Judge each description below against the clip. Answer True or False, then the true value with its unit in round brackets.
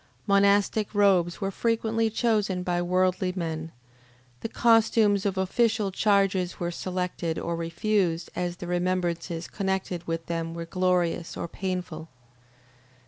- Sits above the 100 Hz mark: True (185 Hz)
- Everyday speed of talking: False (125 wpm)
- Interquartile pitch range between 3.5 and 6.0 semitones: False (2.7 semitones)